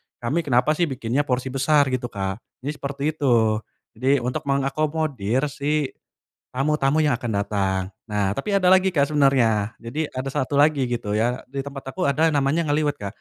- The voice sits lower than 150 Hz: Yes, low, 135 Hz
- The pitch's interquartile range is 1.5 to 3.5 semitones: No, average, 4.0 semitones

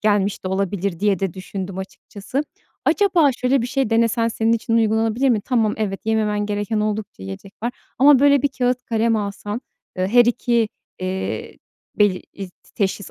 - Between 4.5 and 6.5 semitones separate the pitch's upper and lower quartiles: No, average, 3.3 semitones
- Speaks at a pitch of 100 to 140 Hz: No, high, 215 Hz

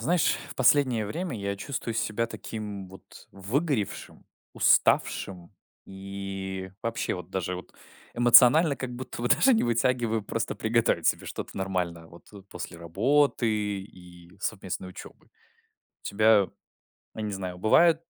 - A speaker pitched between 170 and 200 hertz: No, low, 105 Hz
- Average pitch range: Yes, average, 4.2 semitones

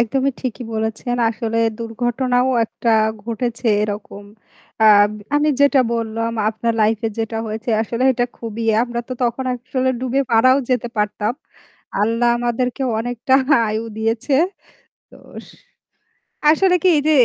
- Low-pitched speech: No, high, 235 Hz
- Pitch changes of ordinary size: No, narrow, 2.2 semitones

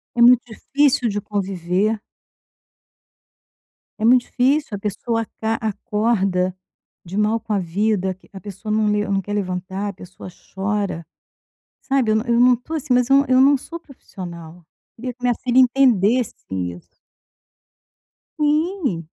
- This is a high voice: Yes, high, 215 Hz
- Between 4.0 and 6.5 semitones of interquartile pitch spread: Yes, average, 4.5 semitones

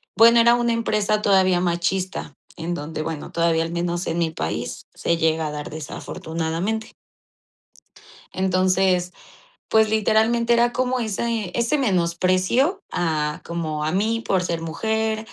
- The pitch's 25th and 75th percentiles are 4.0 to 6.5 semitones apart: Yes, average, 5.0 semitones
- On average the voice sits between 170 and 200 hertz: Yes, medium, 185 Hz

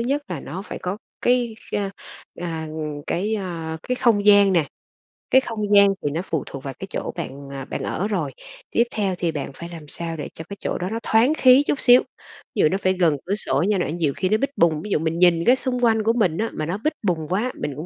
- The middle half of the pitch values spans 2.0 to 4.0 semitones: No, average, 5.2 semitones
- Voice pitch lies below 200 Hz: Yes, medium, 185 Hz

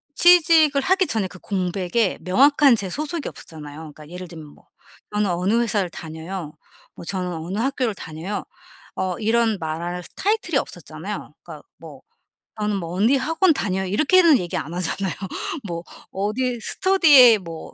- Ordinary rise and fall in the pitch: No, wide, 7.2 semitones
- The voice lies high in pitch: Yes, high, 200 Hz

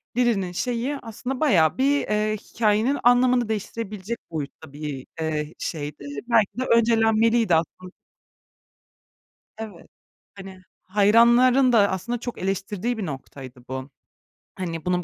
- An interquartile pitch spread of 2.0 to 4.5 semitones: No, wide, 5.4 semitones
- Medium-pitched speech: No, high, 210 Hz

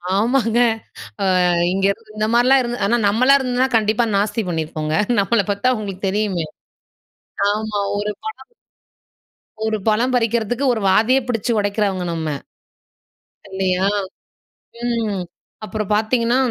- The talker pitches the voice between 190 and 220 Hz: Yes, high, 215 Hz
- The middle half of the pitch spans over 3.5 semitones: No, average, 3.2 semitones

